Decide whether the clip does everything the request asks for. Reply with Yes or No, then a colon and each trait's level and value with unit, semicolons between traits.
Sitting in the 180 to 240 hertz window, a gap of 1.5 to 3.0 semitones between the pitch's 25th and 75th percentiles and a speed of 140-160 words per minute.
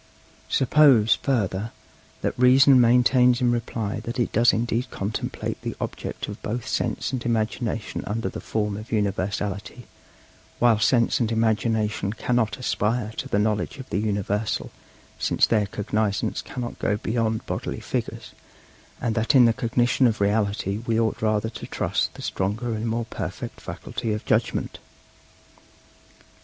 No: low, 110 Hz; narrow, 2.4 semitones; average, 145 wpm